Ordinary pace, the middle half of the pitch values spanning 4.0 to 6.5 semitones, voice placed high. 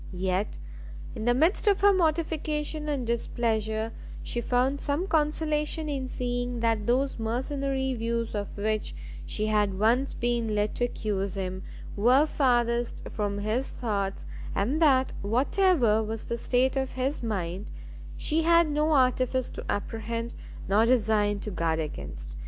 Yes: average, 145 wpm; average, 4.6 semitones; high, 235 Hz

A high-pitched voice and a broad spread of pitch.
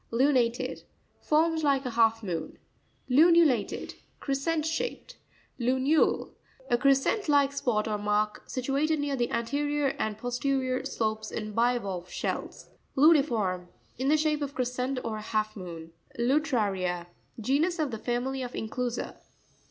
No: very high, 250 Hz; average, 4.8 semitones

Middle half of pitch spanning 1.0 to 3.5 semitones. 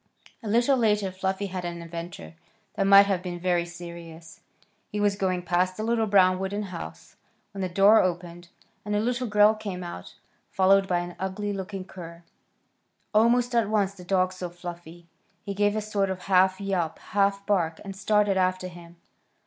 Yes: average, 2.7 semitones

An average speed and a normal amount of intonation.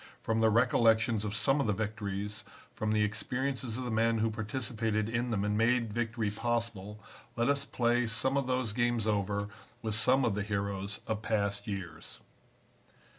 No: average, 175 wpm; narrow, 2.3 semitones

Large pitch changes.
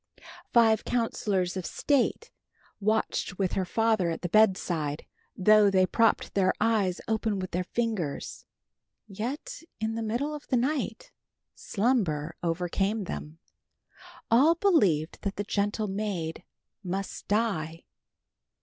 No: average, 3.9 semitones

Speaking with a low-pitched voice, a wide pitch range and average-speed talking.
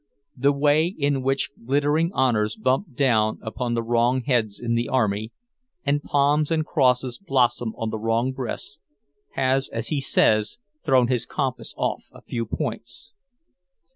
No: low, 130 Hz; average, 3.4 semitones; average, 150 wpm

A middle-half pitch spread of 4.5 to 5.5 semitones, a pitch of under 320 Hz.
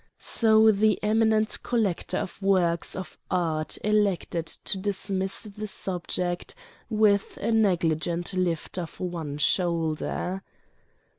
No: average, 3.7 semitones; high, 190 Hz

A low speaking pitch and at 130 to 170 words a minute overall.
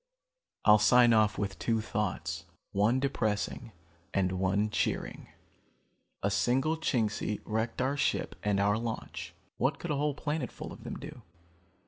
Yes: low, 110 Hz; average, 140 wpm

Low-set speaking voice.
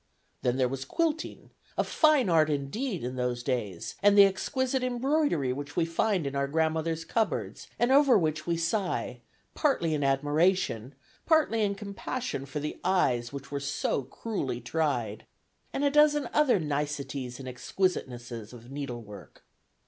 No: medium, 155 Hz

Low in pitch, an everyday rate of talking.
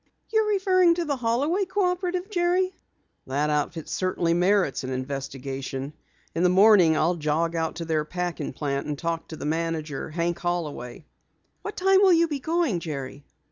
No: medium, 170 Hz; average, 165 wpm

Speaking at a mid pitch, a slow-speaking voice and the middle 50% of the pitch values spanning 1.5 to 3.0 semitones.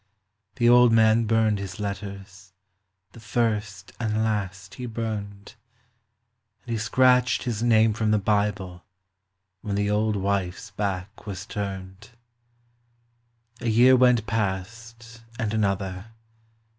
No: low, 105 Hz; slow, 120 wpm; narrow, 2.5 semitones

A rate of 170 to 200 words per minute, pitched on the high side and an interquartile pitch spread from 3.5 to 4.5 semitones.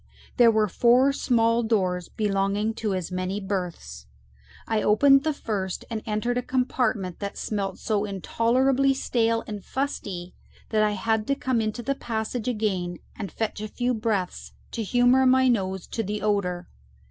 No: average, 160 wpm; high, 215 Hz; average, 3.8 semitones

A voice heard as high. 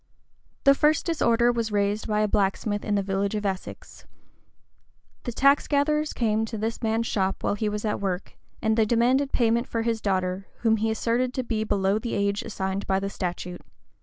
Yes: high, 215 Hz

